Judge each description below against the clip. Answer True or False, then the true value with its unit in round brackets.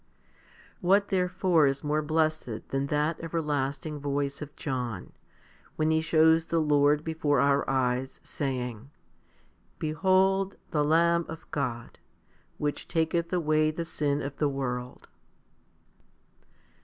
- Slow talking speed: True (120 wpm)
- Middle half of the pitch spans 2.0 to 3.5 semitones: True (2.7 semitones)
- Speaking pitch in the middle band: True (150 Hz)